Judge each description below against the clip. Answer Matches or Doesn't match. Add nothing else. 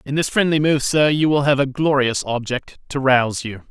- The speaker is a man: Matches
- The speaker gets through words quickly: Matches